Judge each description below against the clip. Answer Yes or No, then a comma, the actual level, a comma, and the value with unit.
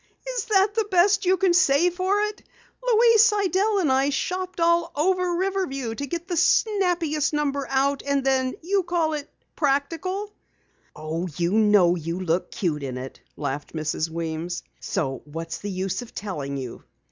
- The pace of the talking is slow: No, average, 165 wpm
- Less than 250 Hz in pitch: No, very high, 290 Hz